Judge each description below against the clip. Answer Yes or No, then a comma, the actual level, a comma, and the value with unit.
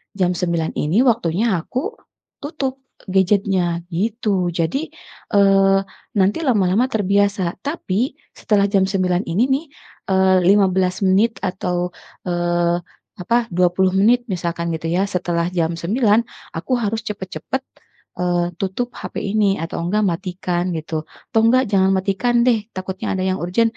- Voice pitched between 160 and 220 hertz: Yes, high, 190 Hz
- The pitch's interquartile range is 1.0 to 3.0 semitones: No, average, 3.5 semitones